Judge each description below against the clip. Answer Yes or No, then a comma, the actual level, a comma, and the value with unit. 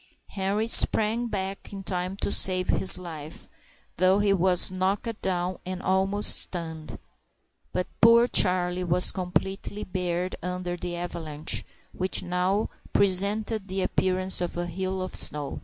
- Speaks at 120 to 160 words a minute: Yes, average, 140 wpm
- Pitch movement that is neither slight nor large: No, narrow, 1.6 semitones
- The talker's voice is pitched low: No, medium, 185 Hz